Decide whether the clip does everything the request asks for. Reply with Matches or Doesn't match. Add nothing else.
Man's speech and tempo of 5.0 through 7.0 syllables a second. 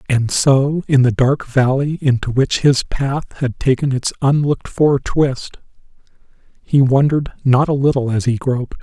Doesn't match